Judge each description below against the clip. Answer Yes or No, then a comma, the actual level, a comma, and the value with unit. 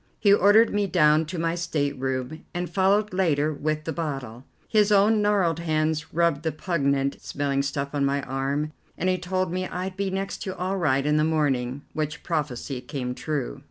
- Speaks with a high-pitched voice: No, medium, 155 Hz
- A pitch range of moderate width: Yes, average, 4.6 semitones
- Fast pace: No, average, 185 wpm